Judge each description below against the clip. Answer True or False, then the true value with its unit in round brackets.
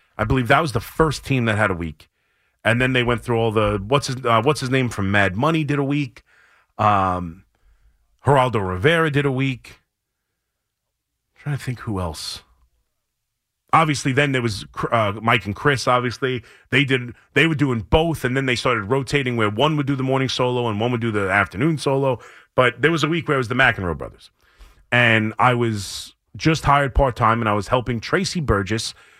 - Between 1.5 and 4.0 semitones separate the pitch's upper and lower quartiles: False (4.5 semitones)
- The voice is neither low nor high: False (125 Hz)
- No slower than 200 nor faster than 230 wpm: True (205 wpm)